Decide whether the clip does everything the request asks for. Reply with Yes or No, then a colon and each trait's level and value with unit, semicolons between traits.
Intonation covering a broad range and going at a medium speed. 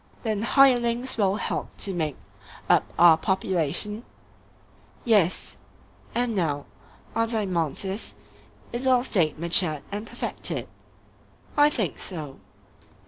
No: wide, 5.8 semitones; slow, 100 wpm